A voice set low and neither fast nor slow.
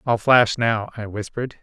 Yes: low, 115 Hz; average, 185 wpm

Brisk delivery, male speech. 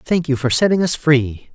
Yes: fast, 235 wpm; male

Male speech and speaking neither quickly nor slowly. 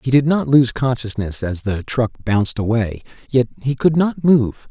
Yes: male; average, 190 wpm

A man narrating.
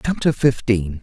Yes: male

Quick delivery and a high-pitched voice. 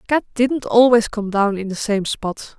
Yes: fast, 210 wpm; high, 220 Hz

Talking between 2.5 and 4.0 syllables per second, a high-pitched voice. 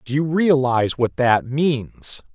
No: 3.7 syllables/s; low, 135 Hz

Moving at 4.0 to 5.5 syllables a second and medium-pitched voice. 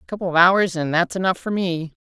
No: 6.0 syllables/s; medium, 180 Hz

